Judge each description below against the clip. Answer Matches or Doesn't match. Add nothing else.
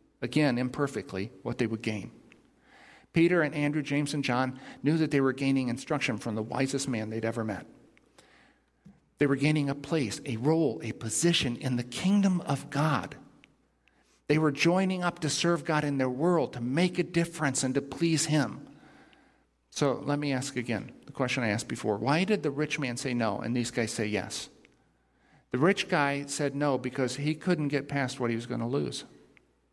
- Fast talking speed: Doesn't match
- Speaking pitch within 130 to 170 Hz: Matches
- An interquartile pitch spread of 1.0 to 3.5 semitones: Doesn't match